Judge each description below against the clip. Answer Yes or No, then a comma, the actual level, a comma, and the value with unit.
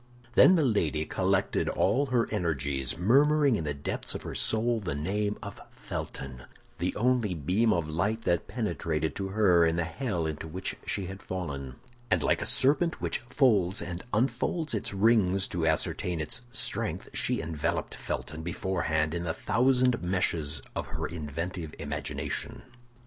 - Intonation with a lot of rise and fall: Yes, wide, 5.9 semitones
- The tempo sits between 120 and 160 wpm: Yes, average, 155 wpm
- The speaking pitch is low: Yes, very low, 90 Hz